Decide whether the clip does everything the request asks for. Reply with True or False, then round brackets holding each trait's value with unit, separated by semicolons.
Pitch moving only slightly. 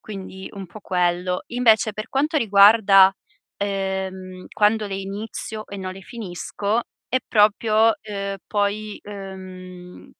True (2.1 semitones)